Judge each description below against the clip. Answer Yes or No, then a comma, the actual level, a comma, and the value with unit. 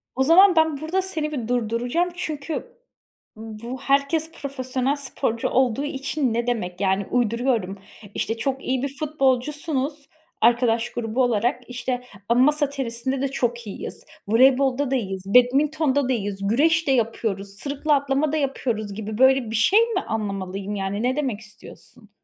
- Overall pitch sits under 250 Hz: No, very high, 255 Hz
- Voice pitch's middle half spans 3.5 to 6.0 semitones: Yes, average, 4.0 semitones